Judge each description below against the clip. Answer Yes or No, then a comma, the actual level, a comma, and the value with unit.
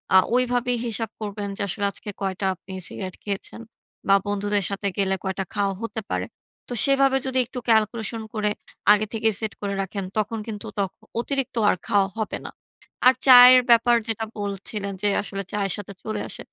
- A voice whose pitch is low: No, high, 210 Hz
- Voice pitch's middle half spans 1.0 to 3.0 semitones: Yes, average, 2.7 semitones